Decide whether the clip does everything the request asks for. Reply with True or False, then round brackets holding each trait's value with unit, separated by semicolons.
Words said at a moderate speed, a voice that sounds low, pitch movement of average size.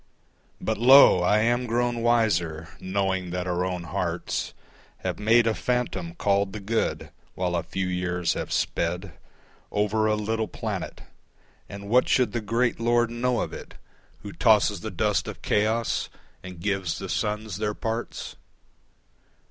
True (150 wpm; 105 Hz; 4.2 semitones)